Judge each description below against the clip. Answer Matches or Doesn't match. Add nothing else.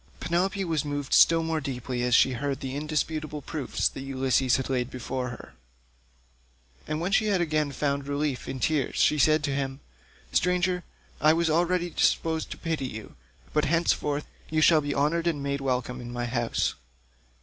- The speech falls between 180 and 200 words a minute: Doesn't match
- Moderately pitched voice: Matches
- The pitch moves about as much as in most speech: Matches